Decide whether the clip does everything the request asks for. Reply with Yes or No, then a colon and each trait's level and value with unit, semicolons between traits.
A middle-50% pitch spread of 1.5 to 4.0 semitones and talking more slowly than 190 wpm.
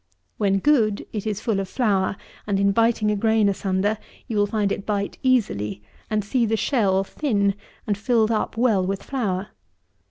Yes: narrow, 2.4 semitones; average, 170 wpm